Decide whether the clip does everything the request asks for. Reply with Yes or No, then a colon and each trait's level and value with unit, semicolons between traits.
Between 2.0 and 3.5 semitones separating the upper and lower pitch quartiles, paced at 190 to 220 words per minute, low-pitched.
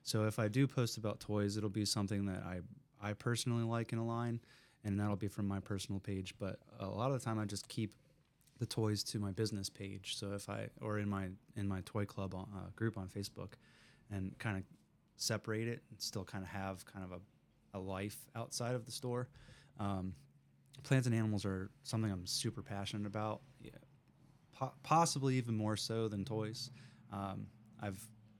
Yes: average, 3.0 semitones; average, 200 wpm; low, 110 Hz